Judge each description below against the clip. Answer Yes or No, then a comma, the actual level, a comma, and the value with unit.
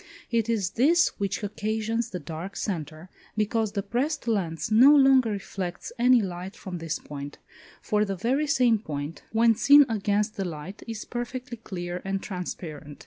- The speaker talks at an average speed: Yes, average, 160 wpm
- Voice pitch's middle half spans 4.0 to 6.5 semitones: Yes, average, 4.6 semitones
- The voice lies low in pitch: No, high, 210 Hz